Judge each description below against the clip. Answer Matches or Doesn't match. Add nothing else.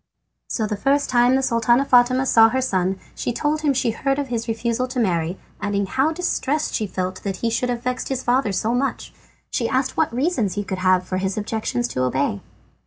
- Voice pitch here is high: Matches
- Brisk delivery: Matches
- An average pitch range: Matches